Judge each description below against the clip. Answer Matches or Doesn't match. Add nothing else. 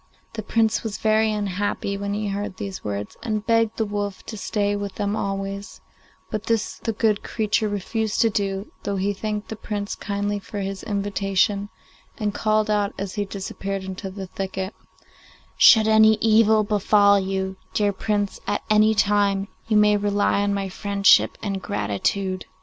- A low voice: Doesn't match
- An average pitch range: Doesn't match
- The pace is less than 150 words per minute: Doesn't match